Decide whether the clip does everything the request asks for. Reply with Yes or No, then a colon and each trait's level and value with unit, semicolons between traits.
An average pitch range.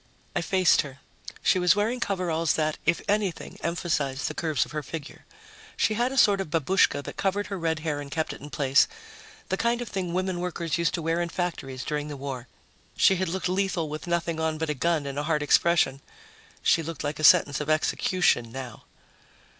Yes: average, 3.8 semitones